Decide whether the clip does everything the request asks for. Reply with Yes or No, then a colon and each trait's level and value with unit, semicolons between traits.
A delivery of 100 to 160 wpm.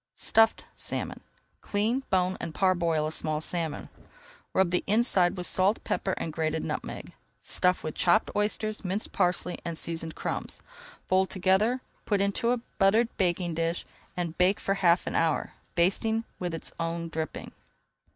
Yes: average, 150 wpm